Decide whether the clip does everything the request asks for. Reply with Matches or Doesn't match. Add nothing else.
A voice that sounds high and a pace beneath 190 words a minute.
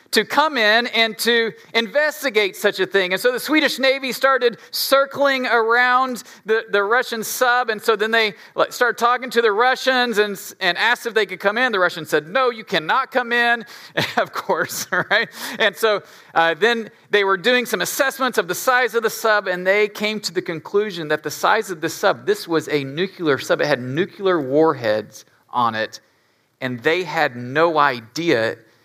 Doesn't match